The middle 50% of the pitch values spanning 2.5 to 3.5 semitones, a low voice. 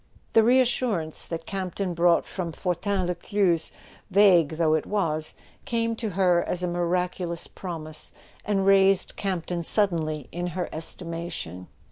No: average, 2.9 semitones; medium, 175 Hz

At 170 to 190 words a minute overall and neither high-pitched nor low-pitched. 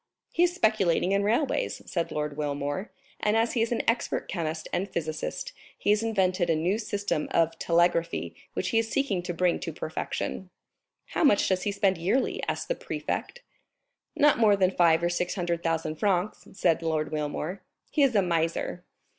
Yes: average, 180 wpm; medium, 180 Hz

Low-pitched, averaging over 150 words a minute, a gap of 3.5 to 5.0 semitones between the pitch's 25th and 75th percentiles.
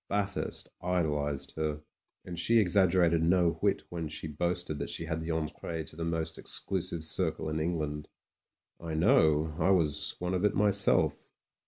No: very low, 85 Hz; average, 160 wpm; narrow, 2.4 semitones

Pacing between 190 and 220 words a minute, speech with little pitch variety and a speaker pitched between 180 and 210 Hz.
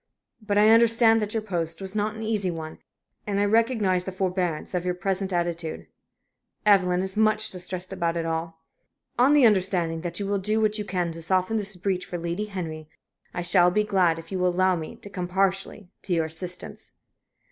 No: average, 200 wpm; average, 3.1 semitones; medium, 185 Hz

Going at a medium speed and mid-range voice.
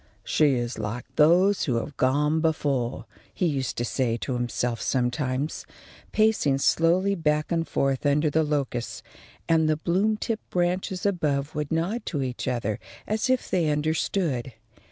Yes: average, 155 wpm; medium, 150 Hz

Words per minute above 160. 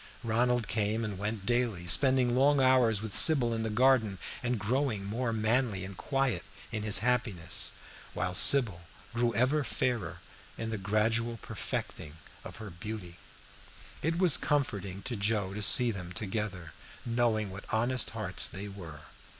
No: average, 150 wpm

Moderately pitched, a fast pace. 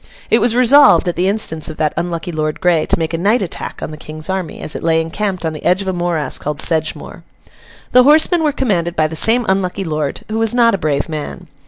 Yes: medium, 175 Hz; fast, 240 wpm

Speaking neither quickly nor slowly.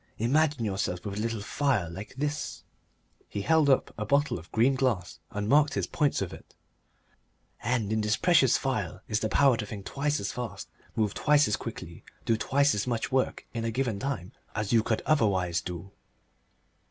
Yes: average, 190 wpm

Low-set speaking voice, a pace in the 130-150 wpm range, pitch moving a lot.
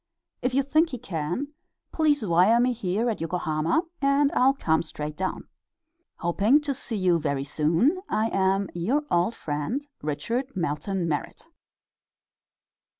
No: high, 195 Hz; average, 140 wpm; wide, 7.8 semitones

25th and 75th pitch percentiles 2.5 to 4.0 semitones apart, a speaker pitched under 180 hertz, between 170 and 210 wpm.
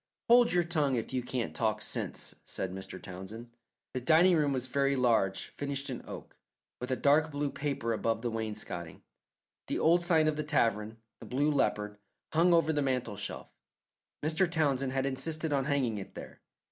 No: average, 5.3 semitones; low, 135 Hz; average, 180 wpm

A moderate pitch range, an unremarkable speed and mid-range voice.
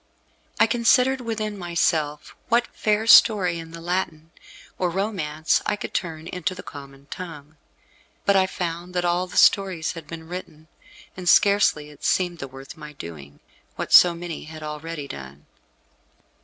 Yes: average, 3.6 semitones; average, 155 wpm; medium, 170 Hz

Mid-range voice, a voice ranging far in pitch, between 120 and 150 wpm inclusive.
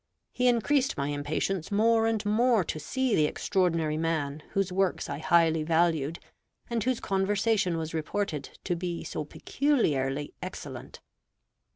Yes: medium, 175 Hz; wide, 5.9 semitones; average, 140 wpm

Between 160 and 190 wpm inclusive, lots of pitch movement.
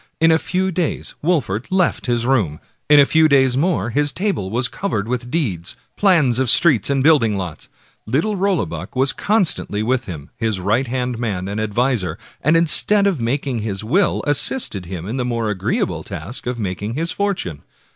Yes: average, 175 wpm; wide, 7.0 semitones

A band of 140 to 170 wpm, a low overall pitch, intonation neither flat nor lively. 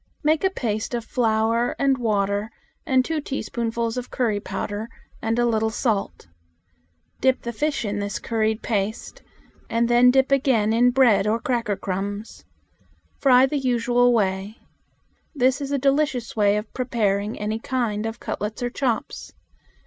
No: average, 155 wpm; high, 230 Hz; average, 3.1 semitones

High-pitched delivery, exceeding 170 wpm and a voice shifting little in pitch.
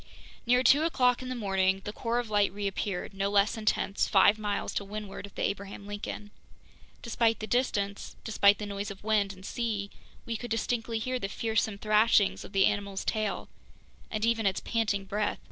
Yes: high, 210 Hz; average, 185 wpm; narrow, 2.2 semitones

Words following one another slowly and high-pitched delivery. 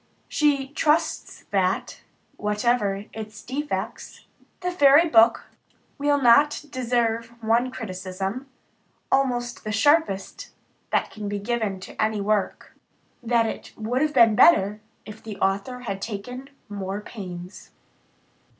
Yes: slow, 120 wpm; high, 225 Hz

